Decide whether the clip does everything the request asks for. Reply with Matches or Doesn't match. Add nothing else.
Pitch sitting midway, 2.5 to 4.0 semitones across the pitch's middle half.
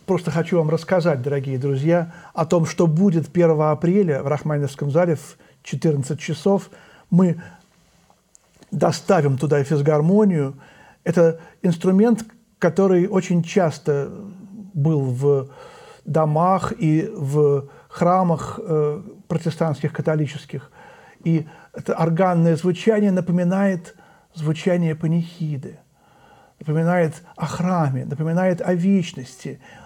Matches